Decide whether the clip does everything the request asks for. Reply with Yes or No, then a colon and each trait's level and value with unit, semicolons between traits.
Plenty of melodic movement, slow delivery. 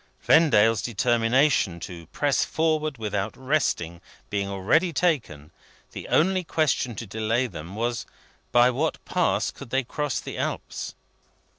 Yes: wide, 6.8 semitones; slow, 130 wpm